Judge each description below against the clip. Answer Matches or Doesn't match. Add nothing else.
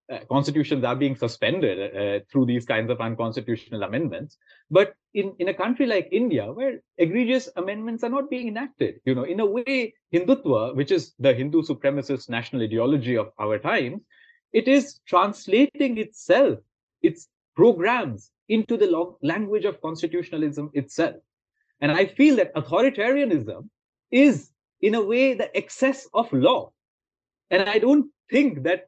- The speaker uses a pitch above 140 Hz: Matches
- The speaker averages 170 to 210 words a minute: Doesn't match